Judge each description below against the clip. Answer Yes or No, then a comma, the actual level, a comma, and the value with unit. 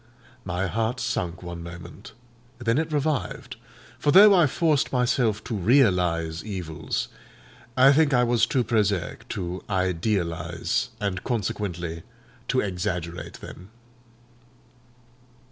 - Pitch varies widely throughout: Yes, wide, 6.1 semitones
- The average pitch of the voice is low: Yes, low, 100 Hz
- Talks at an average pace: No, slow, 110 wpm